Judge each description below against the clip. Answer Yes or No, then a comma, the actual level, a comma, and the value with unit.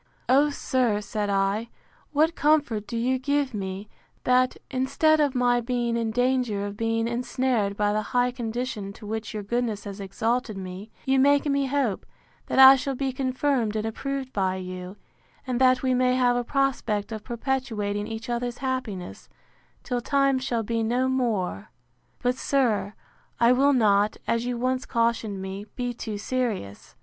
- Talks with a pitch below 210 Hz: No, high, 240 Hz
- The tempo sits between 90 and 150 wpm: No, average, 165 wpm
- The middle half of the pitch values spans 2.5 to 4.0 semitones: Yes, average, 3.7 semitones